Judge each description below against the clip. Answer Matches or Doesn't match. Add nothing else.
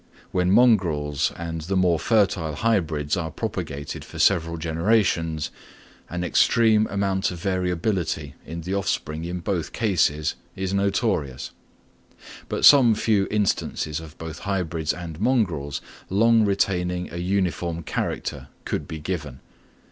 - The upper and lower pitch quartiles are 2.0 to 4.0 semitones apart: Matches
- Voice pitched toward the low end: Matches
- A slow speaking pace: Matches